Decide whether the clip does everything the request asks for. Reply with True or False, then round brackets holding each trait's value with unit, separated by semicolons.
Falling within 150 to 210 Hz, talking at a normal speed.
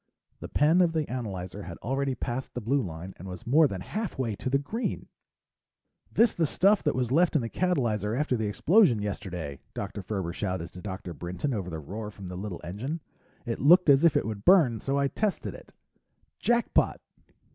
False (120 Hz; 195 wpm)